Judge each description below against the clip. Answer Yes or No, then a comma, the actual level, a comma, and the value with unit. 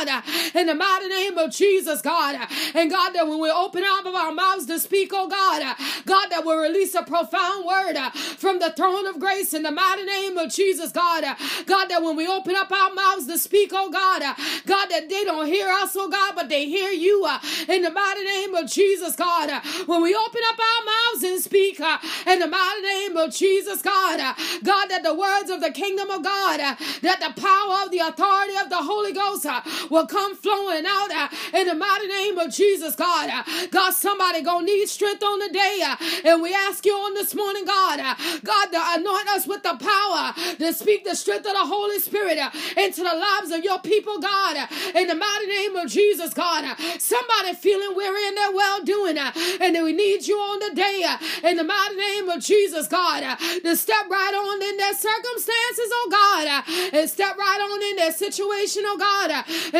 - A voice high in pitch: Yes, very high, 375 Hz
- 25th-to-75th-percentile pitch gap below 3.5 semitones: Yes, average, 3.0 semitones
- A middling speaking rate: No, fast, 215 wpm